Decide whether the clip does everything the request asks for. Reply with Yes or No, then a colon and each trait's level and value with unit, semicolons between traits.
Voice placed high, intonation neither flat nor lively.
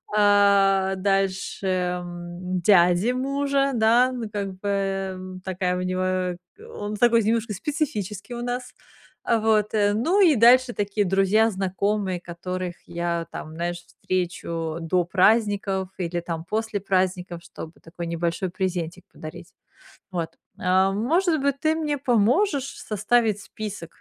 Yes: high, 195 Hz; average, 3.8 semitones